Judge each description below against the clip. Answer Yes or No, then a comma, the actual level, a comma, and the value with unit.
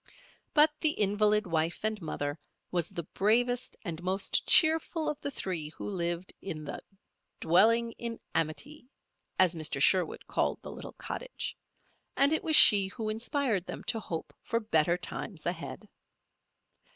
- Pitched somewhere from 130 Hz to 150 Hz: No, high, 200 Hz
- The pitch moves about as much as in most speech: No, wide, 5.7 semitones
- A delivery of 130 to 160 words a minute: Yes, average, 150 wpm